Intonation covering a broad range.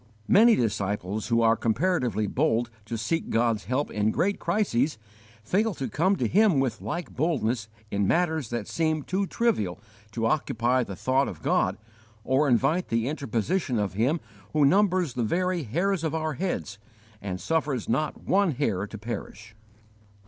Yes: wide, 7.2 semitones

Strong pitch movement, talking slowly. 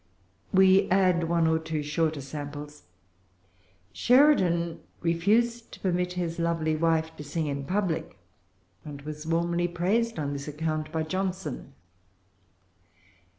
No: average, 2.9 semitones; slow, 120 wpm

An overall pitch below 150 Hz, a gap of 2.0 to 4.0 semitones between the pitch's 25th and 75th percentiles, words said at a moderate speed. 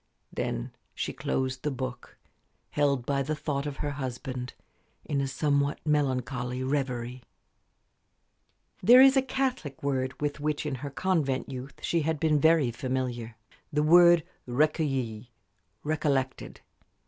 No: medium, 140 Hz; average, 2.8 semitones; slow, 130 wpm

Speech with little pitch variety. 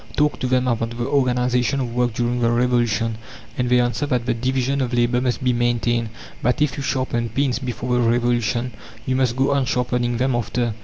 Yes: narrow, 1.3 semitones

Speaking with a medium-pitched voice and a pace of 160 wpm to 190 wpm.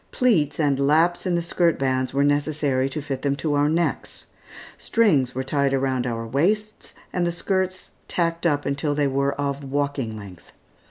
Yes: medium, 145 Hz; average, 175 wpm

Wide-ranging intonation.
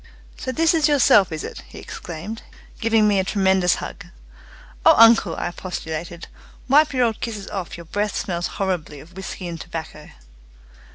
No: average, 4.9 semitones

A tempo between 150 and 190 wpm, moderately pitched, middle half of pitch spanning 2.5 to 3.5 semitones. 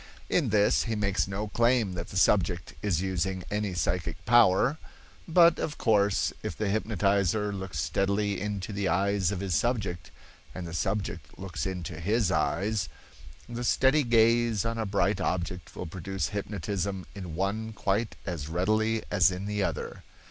No: average, 160 wpm; low, 100 Hz; average, 3.0 semitones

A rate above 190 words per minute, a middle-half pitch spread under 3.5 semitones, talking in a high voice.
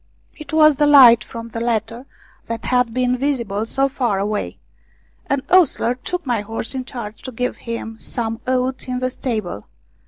No: average, 175 wpm; narrow, 2.6 semitones; high, 245 Hz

